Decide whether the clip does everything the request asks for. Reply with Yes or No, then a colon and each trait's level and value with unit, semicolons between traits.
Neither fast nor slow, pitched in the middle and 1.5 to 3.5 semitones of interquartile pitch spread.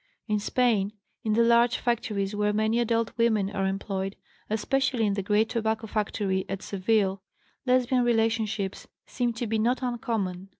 No: average, 155 wpm; high, 220 Hz; average, 2.8 semitones